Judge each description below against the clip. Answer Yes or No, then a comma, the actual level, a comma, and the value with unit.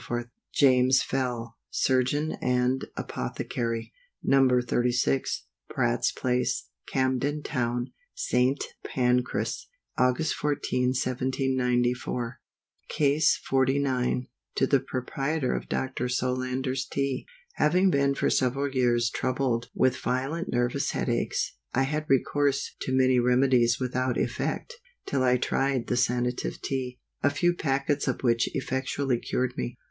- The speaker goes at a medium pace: No, slow, 115 wpm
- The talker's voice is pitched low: Yes, low, 130 Hz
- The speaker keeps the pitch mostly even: Yes, narrow, 1.7 semitones